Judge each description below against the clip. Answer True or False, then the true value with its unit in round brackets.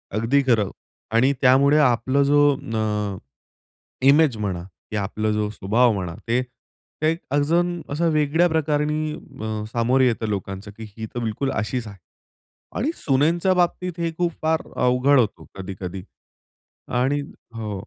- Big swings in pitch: True (5.8 semitones)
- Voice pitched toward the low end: True (125 Hz)